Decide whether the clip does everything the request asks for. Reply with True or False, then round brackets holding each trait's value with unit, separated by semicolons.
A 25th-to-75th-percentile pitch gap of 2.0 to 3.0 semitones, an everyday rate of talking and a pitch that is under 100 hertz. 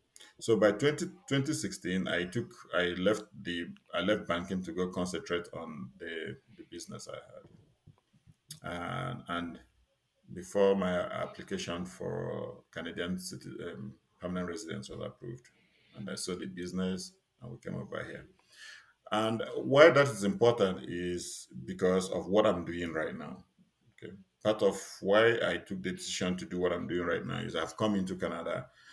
True (2.7 semitones; 160 wpm; 90 Hz)